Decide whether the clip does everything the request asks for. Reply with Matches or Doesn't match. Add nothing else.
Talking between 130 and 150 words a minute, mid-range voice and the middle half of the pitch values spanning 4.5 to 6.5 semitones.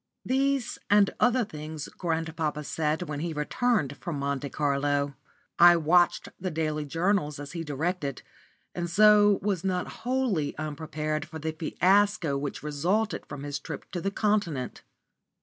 Matches